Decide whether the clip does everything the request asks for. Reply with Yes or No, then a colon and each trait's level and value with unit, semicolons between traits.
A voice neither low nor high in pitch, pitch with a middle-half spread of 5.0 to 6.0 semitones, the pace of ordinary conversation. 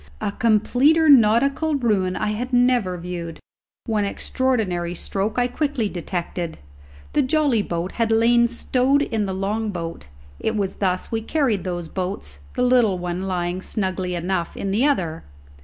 No: high, 210 Hz; average, 5.3 semitones; average, 155 wpm